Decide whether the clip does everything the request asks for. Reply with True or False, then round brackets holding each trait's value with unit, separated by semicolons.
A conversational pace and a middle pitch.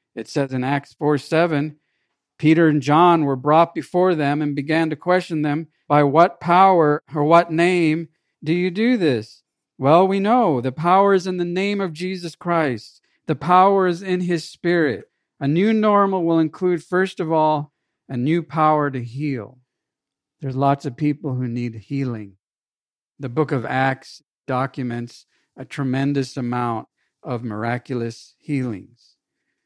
True (155 wpm; 150 Hz)